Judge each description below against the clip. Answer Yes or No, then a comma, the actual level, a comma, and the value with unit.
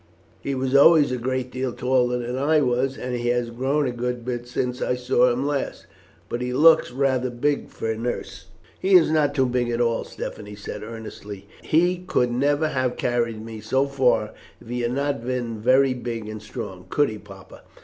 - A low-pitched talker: Yes, low, 125 Hz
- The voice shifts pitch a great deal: No, narrow, 2.4 semitones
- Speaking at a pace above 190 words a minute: Yes, average, 200 wpm